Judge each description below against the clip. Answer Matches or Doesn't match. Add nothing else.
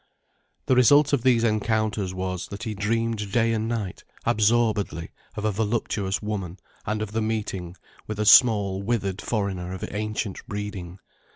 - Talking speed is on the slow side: Doesn't match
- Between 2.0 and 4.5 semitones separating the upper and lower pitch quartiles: Matches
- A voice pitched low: Matches